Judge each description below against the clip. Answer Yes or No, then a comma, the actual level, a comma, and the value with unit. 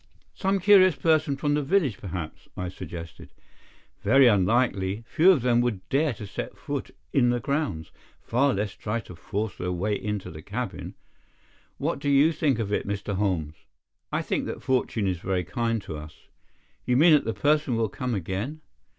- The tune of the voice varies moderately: No, wide, 6.5 semitones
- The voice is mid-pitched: No, low, 115 Hz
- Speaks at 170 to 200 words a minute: Yes, average, 180 wpm